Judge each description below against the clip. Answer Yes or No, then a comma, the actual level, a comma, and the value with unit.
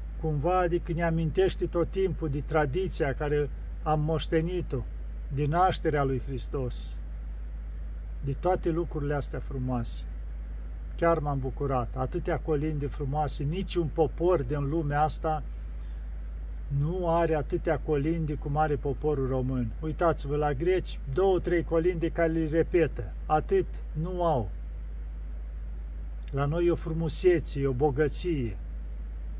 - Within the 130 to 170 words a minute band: No, average, 120 wpm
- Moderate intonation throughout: No, wide, 6.2 semitones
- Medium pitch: Yes, medium, 150 Hz